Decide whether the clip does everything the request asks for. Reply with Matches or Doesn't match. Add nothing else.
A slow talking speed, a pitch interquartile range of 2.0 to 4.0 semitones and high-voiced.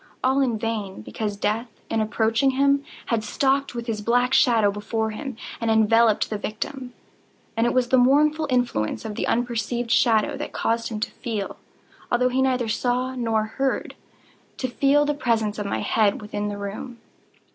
Doesn't match